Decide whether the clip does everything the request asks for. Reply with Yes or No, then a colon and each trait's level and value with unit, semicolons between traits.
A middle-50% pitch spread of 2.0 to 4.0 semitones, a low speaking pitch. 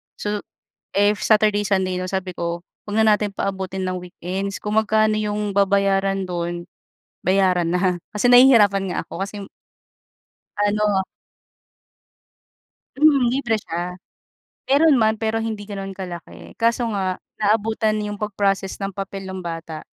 No: narrow, 2.4 semitones; high, 200 Hz